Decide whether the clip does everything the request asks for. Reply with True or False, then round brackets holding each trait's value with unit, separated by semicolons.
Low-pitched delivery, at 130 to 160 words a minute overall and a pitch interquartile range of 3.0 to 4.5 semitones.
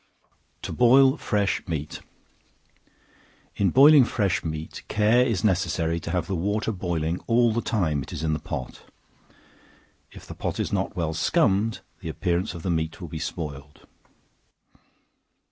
False (90 Hz; 150 wpm; 5.5 semitones)